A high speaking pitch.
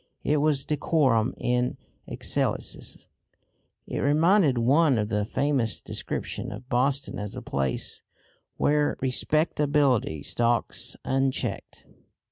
No: low, 135 Hz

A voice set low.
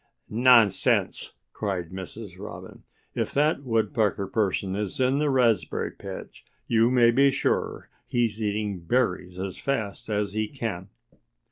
Yes: low, 105 Hz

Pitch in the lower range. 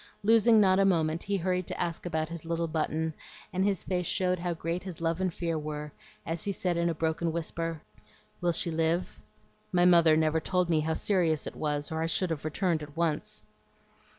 No: medium, 165 Hz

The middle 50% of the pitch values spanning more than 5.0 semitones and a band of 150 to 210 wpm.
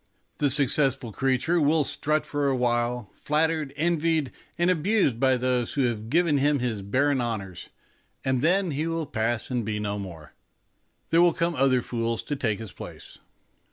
No: average, 4.7 semitones; average, 170 wpm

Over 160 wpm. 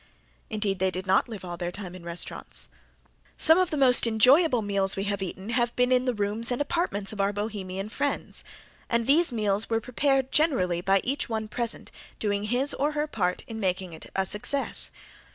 Yes: average, 195 wpm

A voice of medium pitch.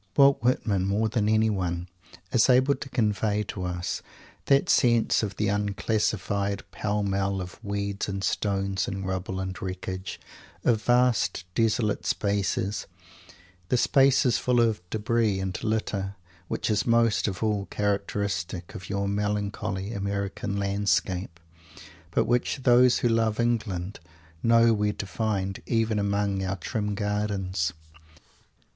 No: low, 105 Hz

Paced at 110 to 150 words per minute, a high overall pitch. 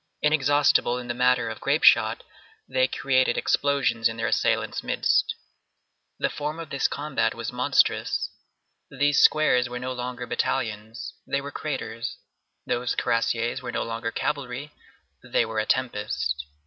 No: average, 145 wpm; low, 125 Hz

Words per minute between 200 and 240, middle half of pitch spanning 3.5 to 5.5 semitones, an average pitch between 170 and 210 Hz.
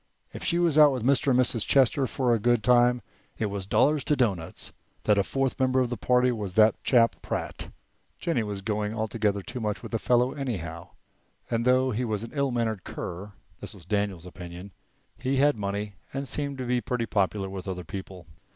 No: fast, 205 wpm; average, 4.2 semitones; low, 115 Hz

